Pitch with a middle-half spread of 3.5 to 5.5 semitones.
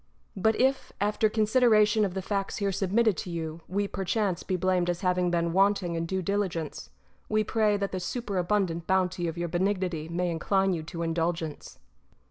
No: average, 3.1 semitones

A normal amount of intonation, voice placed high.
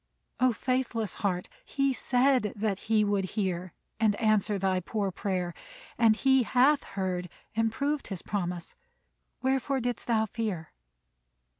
Yes: average, 4.5 semitones; high, 215 Hz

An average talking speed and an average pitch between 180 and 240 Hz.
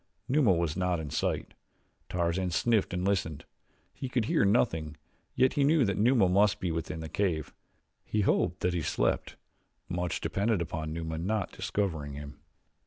No: average, 165 wpm; very low, 90 Hz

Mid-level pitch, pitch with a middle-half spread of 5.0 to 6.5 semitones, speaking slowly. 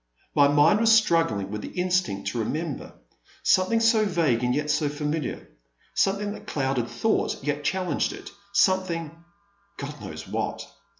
No: medium, 160 Hz; wide, 5.5 semitones; average, 165 wpm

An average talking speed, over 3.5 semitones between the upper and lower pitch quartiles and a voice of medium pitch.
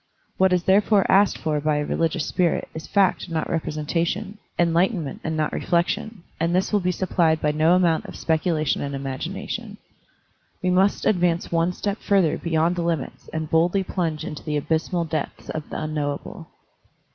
No: average, 175 wpm; average, 2.7 semitones; medium, 165 Hz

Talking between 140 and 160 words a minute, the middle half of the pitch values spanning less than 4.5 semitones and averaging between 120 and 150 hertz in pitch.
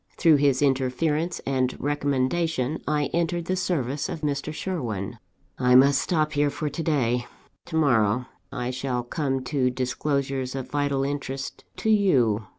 Yes: average, 150 wpm; average, 3.1 semitones; medium, 140 Hz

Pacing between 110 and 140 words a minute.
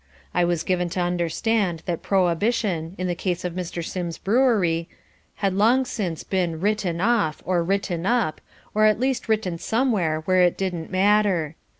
No: average, 165 wpm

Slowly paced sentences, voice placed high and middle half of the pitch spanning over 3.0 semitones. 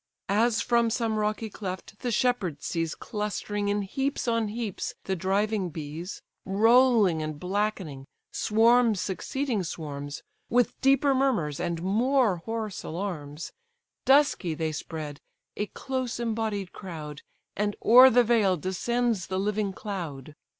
Yes: slow, 130 wpm; high, 205 Hz; average, 5.2 semitones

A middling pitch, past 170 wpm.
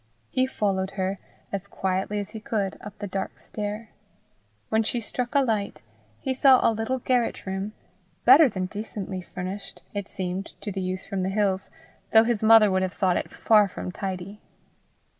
No: high, 205 Hz; average, 180 wpm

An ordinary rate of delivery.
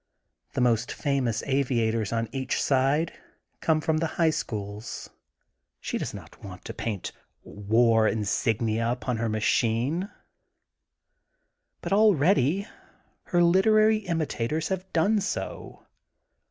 No: slow, 115 wpm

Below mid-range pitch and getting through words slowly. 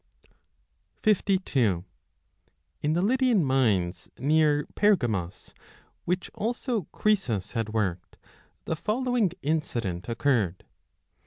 No: medium, 145 Hz; slow, 85 wpm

